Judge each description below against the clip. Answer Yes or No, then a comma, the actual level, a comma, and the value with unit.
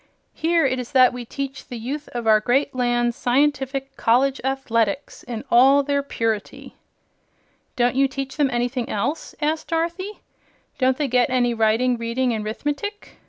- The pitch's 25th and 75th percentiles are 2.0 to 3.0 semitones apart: Yes, average, 2.7 semitones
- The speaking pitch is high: Yes, very high, 255 Hz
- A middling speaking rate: Yes, average, 160 wpm